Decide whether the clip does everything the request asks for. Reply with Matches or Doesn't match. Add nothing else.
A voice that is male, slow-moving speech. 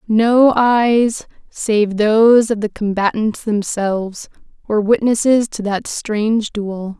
Doesn't match